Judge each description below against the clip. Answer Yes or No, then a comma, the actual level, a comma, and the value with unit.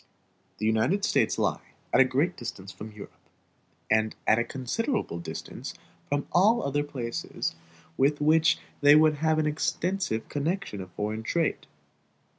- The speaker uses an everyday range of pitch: No, wide, 6.6 semitones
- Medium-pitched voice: Yes, medium, 145 Hz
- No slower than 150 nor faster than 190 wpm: No, average, 140 wpm